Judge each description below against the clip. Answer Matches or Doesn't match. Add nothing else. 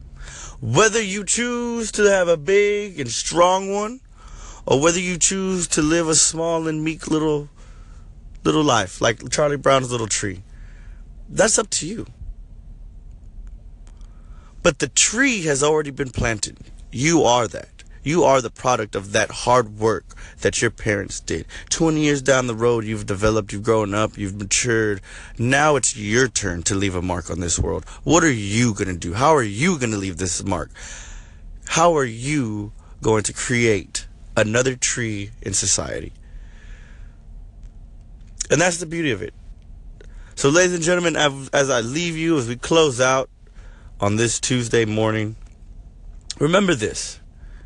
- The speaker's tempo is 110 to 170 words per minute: Matches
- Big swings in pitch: Matches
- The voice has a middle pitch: Doesn't match